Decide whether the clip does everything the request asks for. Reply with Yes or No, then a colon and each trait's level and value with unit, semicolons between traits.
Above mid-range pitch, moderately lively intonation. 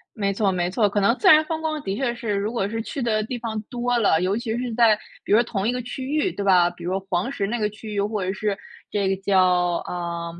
Yes: high, 210 Hz; average, 3.6 semitones